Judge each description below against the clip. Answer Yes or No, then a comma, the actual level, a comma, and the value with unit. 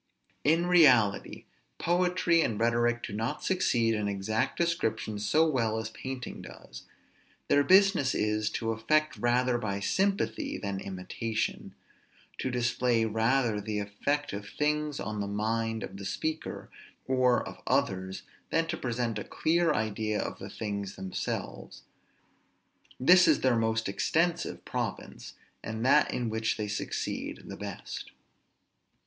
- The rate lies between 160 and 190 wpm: No, slow, 135 wpm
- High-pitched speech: No, low, 115 Hz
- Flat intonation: No, wide, 5.4 semitones